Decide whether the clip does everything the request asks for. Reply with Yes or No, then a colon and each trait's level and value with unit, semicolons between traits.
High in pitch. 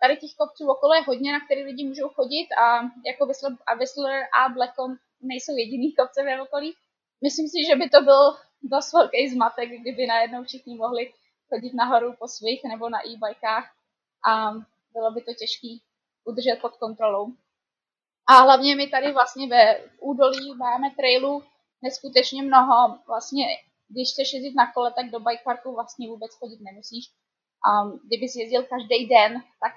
Yes: very high, 255 Hz